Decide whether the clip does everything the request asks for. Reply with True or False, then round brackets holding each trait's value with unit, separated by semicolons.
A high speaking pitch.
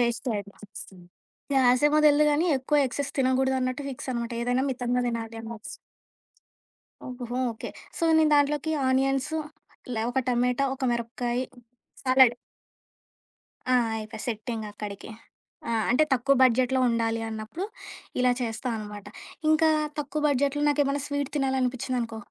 True (250 Hz)